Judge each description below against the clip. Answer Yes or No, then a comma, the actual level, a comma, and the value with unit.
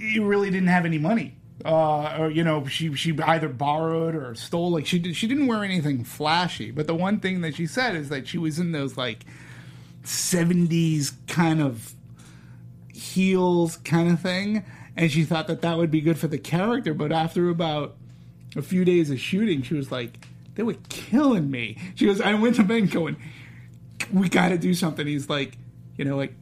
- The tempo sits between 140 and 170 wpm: No, average, 200 wpm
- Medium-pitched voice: Yes, medium, 160 Hz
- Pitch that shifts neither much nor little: Yes, average, 4.5 semitones